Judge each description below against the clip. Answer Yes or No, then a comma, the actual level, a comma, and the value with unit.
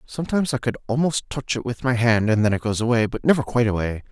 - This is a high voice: No, low, 120 Hz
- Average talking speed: No, fast, 260 wpm